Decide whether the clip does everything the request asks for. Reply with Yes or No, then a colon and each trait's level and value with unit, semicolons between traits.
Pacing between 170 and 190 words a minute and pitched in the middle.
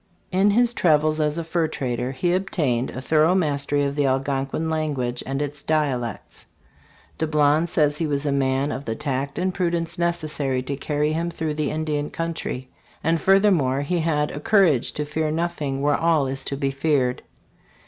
Yes: average, 180 wpm; medium, 150 Hz